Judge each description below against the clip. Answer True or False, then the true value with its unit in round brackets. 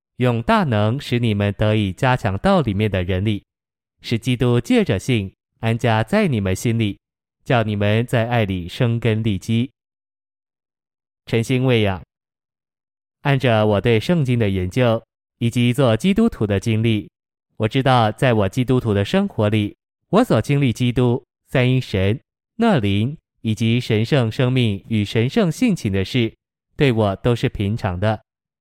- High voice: False (115 Hz)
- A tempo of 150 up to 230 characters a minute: True (220 characters per minute)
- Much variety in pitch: False (3.4 semitones)